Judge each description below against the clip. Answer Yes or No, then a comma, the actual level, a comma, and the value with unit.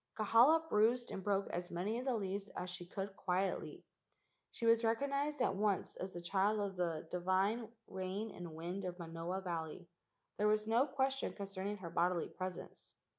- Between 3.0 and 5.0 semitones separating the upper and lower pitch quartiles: Yes, average, 3.8 semitones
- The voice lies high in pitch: Yes, high, 195 Hz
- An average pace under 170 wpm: No, average, 175 wpm